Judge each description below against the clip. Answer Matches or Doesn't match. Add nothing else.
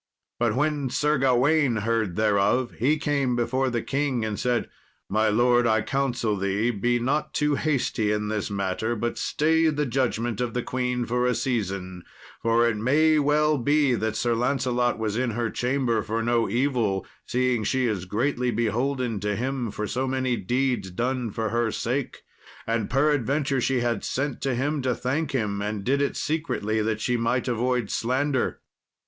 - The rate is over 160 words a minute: Matches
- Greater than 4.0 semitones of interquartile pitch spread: Doesn't match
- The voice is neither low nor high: Doesn't match